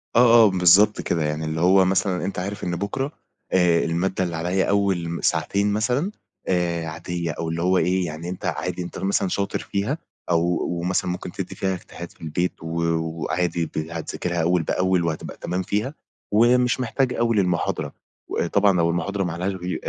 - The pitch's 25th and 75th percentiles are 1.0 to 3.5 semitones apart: Yes, average, 2.8 semitones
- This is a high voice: No, very low, 90 Hz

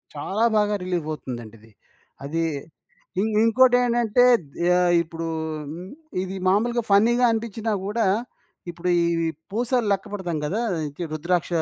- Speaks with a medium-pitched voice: No, high, 200 Hz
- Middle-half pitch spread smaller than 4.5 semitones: No, average, 5.2 semitones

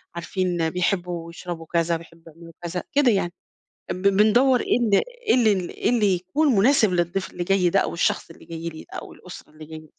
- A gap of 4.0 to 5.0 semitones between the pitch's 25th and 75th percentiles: No, average, 3.2 semitones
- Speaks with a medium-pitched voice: Yes, medium, 180 Hz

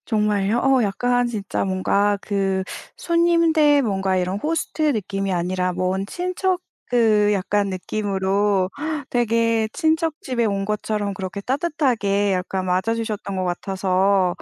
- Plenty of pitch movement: No, average, 4.0 semitones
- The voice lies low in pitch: No, high, 205 Hz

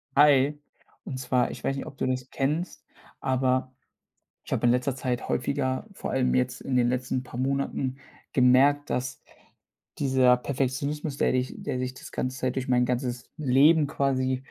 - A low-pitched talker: Yes, low, 130 Hz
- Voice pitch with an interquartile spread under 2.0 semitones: Yes, narrow, 1.4 semitones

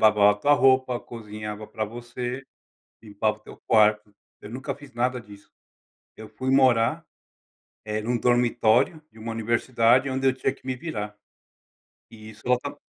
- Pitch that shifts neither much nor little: Yes, average, 3.2 semitones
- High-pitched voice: No, low, 115 Hz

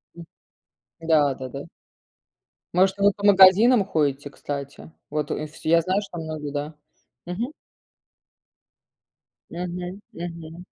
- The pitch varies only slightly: No, average, 4.2 semitones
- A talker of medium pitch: Yes, medium, 170 Hz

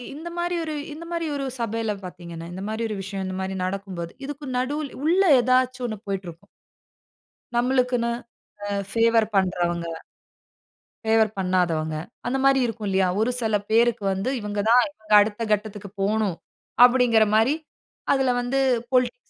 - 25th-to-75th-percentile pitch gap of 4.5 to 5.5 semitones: Yes, average, 4.8 semitones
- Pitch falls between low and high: No, high, 220 Hz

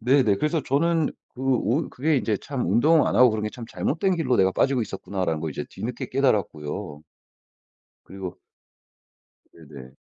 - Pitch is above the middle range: No, low, 120 Hz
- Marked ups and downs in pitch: Yes, wide, 6.7 semitones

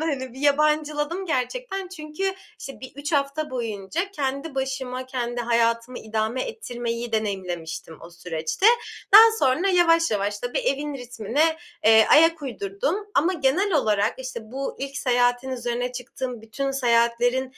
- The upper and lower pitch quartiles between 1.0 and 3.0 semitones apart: No, average, 4.5 semitones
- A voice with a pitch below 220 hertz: No, very high, 260 Hz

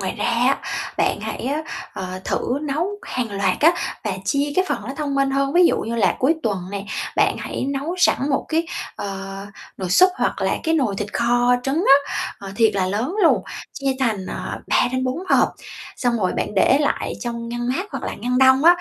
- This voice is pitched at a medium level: No, very high, 255 Hz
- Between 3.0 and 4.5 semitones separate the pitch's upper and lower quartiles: No, average, 5.1 semitones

